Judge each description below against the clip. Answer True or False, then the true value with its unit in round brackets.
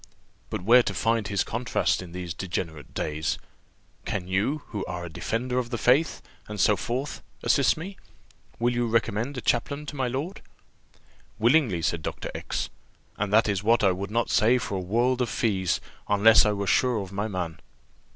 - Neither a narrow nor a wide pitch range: True (4.5 semitones)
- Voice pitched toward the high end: False (110 Hz)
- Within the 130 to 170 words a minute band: False (185 wpm)